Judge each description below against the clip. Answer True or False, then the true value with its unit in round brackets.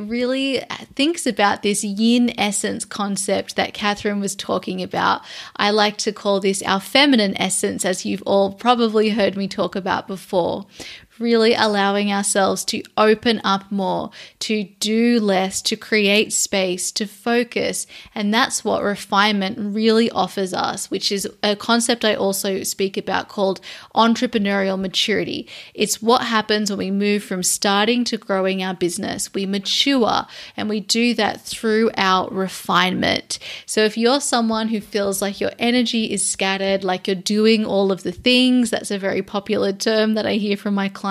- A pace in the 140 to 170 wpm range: True (165 wpm)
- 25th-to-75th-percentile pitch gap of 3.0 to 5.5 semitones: False (2.5 semitones)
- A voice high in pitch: True (205 Hz)